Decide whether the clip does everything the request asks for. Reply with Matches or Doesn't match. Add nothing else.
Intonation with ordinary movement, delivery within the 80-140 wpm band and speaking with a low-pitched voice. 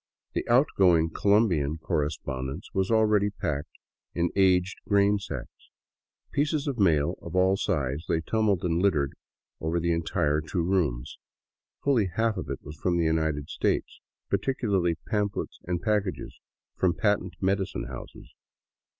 Matches